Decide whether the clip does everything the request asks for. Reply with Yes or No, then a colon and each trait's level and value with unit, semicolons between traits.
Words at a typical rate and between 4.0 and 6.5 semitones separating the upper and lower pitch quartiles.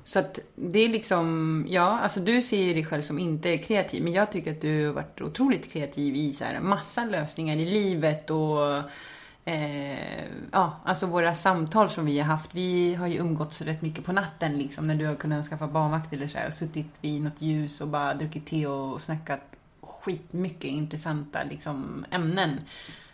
No: average, 185 wpm; average, 3.2 semitones